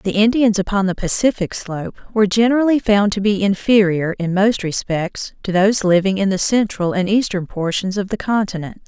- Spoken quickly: No, average, 180 wpm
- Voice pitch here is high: Yes, high, 200 Hz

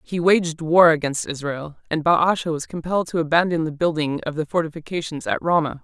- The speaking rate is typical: Yes, average, 185 wpm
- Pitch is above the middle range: No, medium, 160 Hz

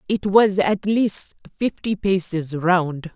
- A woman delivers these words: Yes, female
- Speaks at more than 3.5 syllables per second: No, 3.3 syllables/s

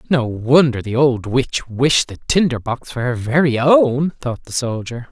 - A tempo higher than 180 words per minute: Yes, average, 190 wpm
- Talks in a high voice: No, low, 130 Hz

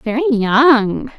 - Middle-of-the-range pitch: No, very high, 250 Hz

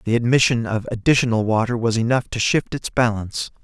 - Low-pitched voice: Yes, low, 115 Hz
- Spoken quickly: No, average, 180 wpm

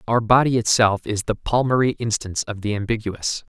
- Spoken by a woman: No, male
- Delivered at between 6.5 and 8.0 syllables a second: No, 5.5 syllables/s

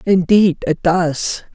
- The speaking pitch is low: No, medium, 175 Hz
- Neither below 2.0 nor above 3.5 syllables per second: Yes, 3.2 syllables/s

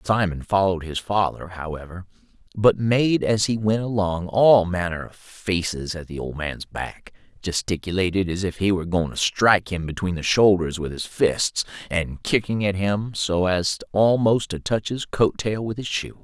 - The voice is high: No, very low, 95 Hz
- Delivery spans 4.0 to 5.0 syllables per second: Yes, 4.6 syllables/s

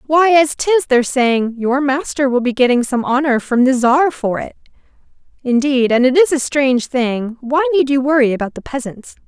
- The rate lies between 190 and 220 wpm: Yes, average, 200 wpm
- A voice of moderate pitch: No, very high, 255 Hz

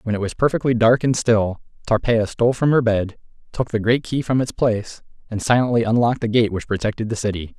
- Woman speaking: No, male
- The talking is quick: Yes, fast, 220 wpm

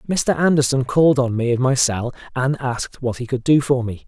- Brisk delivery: Yes, fast, 235 wpm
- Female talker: No, male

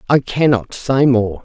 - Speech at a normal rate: Yes, average, 165 wpm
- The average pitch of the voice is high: No, low, 125 Hz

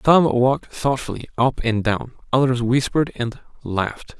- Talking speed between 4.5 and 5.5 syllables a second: Yes, 4.8 syllables/s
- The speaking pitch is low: Yes, low, 125 Hz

